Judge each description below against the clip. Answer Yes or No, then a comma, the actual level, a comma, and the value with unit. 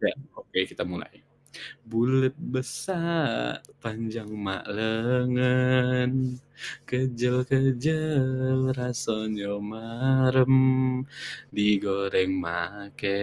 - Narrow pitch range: No, average, 3.2 semitones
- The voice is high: No, low, 125 Hz